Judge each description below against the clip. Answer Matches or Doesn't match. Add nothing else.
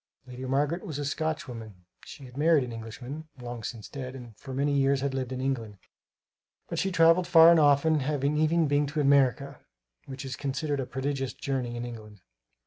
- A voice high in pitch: Doesn't match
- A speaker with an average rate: Matches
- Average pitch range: Matches